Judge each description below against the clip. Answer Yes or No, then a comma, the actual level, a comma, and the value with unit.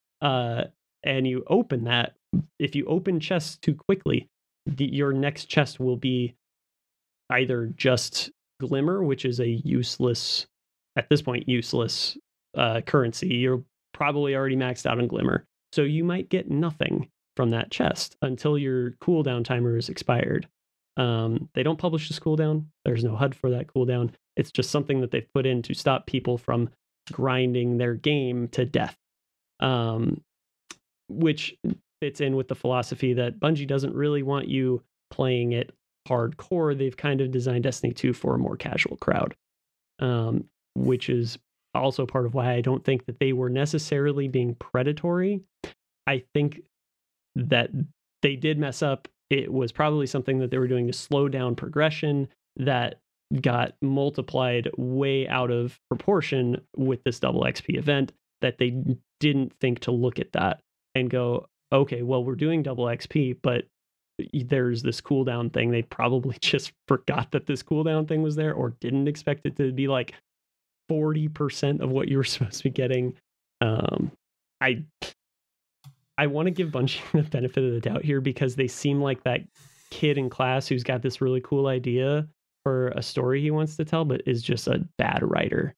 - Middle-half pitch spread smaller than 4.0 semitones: Yes, average, 2.8 semitones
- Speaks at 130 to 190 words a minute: Yes, average, 170 wpm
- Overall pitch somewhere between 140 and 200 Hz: No, low, 130 Hz